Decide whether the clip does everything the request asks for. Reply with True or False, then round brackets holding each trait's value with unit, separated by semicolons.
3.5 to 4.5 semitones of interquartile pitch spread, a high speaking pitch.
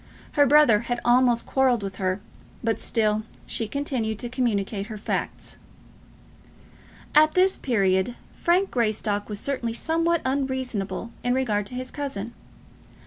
True (4.1 semitones; 240 Hz)